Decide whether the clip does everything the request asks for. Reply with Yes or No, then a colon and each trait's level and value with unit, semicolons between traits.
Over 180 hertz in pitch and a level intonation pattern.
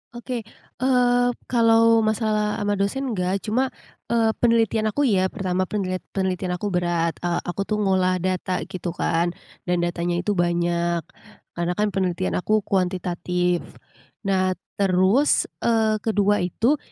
No: high, 190 Hz; average, 3.7 semitones